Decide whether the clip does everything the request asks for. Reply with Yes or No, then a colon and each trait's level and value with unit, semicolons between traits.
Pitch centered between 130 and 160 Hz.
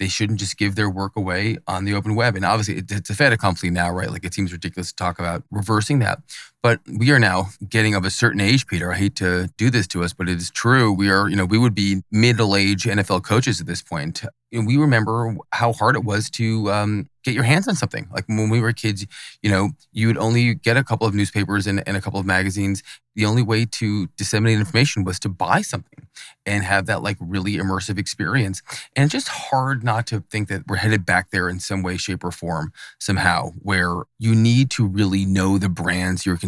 No: low, 105 Hz